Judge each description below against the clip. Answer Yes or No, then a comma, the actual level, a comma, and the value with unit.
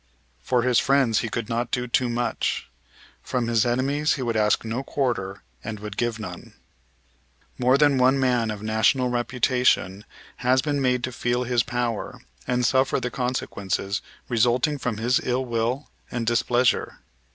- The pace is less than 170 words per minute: Yes, average, 160 wpm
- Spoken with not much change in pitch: Yes, narrow, 2.0 semitones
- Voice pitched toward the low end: Yes, low, 120 Hz